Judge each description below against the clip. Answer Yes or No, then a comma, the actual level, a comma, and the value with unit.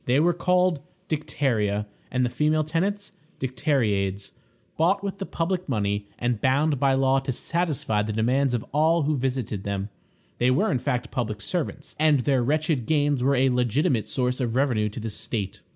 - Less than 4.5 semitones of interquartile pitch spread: No, average, 5.0 semitones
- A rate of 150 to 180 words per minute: Yes, average, 175 wpm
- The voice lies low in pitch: Yes, low, 130 Hz